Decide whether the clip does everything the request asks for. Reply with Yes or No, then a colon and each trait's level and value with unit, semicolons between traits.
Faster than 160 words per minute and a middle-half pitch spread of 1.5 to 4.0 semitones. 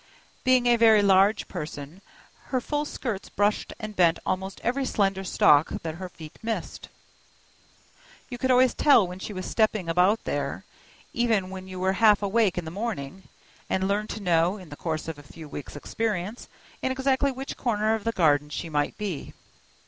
No: average, 180 wpm; average, 4.7 semitones